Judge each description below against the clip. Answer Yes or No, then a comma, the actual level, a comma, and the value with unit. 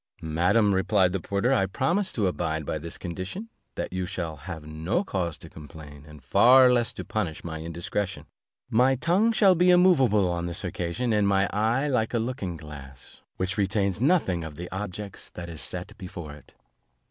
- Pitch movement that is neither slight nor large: No, wide, 5.9 semitones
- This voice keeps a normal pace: Yes, average, 180 wpm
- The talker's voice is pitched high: No, very low, 95 Hz